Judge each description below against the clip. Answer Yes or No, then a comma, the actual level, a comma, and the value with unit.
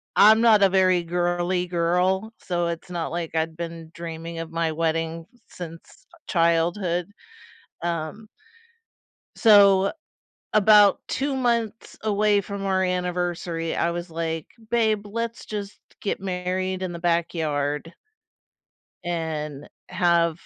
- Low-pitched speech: No, medium, 175 Hz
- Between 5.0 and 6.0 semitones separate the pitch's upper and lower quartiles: No, average, 3.1 semitones